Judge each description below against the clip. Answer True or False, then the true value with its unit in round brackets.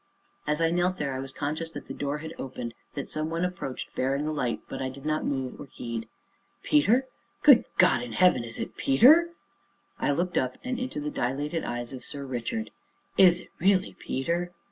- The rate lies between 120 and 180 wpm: False (200 wpm)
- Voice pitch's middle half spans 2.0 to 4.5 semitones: False (5.2 semitones)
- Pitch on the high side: False (150 Hz)